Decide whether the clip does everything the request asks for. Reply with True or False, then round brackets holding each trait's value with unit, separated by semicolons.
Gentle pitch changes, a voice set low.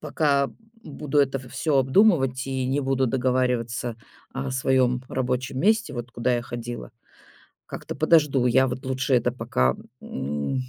True (1.8 semitones; 130 Hz)